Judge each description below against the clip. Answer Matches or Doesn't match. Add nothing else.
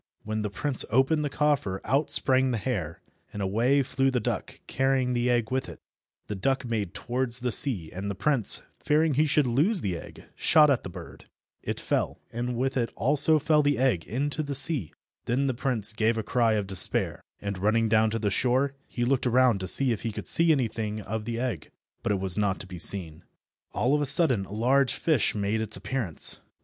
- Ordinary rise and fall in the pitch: Matches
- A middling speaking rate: Doesn't match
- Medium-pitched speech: Doesn't match